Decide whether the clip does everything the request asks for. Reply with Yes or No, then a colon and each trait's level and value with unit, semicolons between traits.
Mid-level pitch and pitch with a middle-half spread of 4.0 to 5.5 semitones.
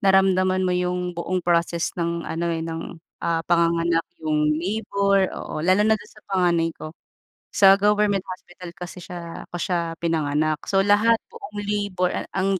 No: medium, 180 Hz; narrow, 2.5 semitones